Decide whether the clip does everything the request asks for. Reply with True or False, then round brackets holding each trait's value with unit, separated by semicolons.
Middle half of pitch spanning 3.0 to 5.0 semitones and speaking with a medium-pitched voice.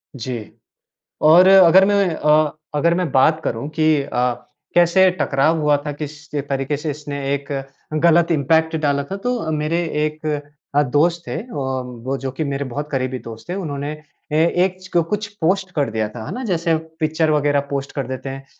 True (3.6 semitones; 150 Hz)